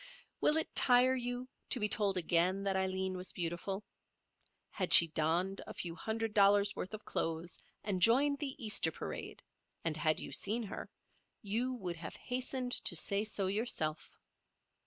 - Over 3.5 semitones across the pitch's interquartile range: Yes, average, 5.1 semitones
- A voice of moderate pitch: No, high, 200 Hz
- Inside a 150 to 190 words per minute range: Yes, average, 160 wpm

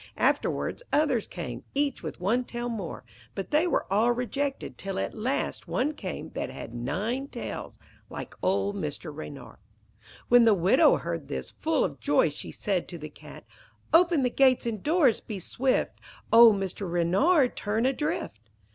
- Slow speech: No, average, 165 wpm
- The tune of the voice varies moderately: No, wide, 6.6 semitones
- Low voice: No, high, 230 Hz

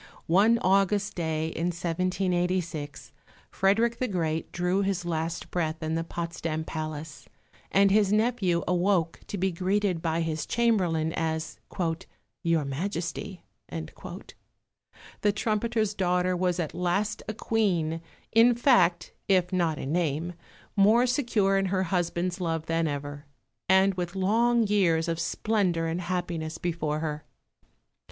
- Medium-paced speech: No, slow, 130 wpm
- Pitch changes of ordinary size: Yes, average, 3.3 semitones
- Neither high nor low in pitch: Yes, medium, 180 Hz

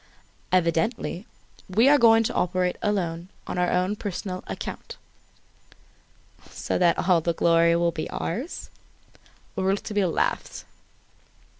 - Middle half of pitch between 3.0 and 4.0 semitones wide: Yes, average, 3.4 semitones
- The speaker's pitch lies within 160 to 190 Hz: Yes, medium, 185 Hz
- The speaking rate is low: Yes, slow, 115 wpm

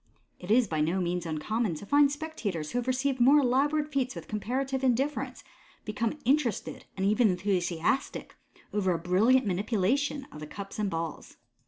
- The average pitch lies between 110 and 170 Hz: No, high, 225 Hz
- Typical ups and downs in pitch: No, wide, 6.5 semitones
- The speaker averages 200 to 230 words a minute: No, average, 165 wpm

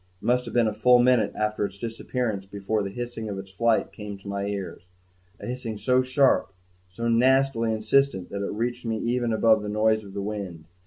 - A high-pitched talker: No, low, 110 Hz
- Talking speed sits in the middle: No, fast, 210 wpm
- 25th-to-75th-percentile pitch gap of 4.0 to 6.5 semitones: No, average, 3.2 semitones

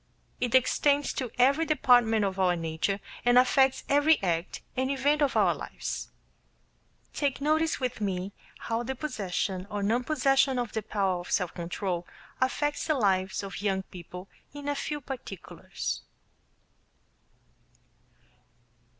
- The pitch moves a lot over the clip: Yes, wide, 6.5 semitones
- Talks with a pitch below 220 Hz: No, high, 240 Hz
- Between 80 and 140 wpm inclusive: Yes, slow, 135 wpm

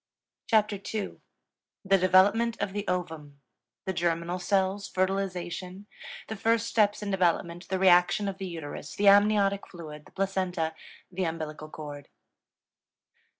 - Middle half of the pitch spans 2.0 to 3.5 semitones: Yes, average, 2.8 semitones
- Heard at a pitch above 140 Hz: Yes, medium, 185 Hz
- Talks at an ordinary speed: No, slow, 130 wpm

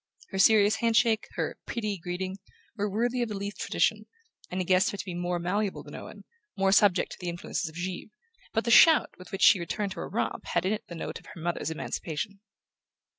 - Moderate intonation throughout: Yes, average, 3.2 semitones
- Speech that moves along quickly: Yes, fast, 220 wpm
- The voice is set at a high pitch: Yes, high, 195 Hz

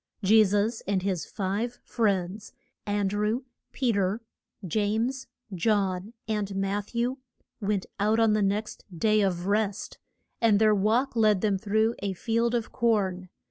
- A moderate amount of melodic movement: No, narrow, 2.2 semitones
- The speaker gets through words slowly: No, average, 150 wpm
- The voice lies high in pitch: Yes, high, 210 Hz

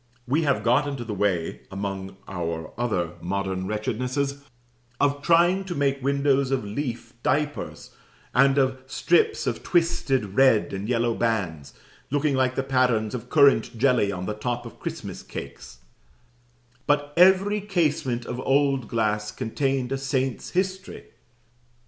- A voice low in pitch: Yes, low, 130 Hz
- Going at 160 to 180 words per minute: No, average, 140 wpm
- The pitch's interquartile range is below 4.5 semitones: No, average, 5.0 semitones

